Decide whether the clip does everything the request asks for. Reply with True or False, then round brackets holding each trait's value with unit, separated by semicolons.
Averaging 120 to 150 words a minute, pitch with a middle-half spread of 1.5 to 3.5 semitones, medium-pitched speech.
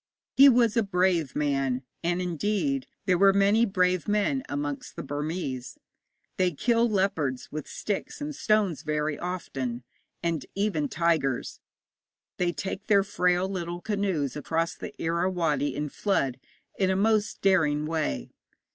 False (140 wpm; 5.1 semitones; 180 Hz)